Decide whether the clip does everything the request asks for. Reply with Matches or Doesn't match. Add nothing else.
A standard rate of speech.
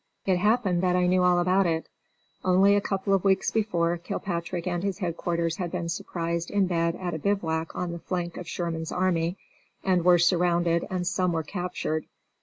Matches